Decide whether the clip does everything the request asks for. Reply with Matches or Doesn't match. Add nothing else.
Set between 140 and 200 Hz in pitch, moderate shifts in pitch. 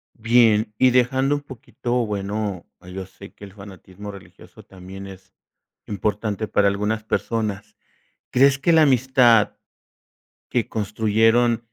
Doesn't match